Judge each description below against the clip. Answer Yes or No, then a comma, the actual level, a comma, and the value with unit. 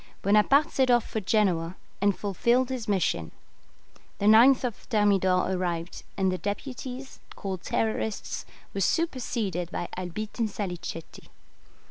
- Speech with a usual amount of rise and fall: Yes, average, 4.6 semitones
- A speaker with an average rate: No, slow, 120 wpm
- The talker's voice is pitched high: Yes, high, 205 Hz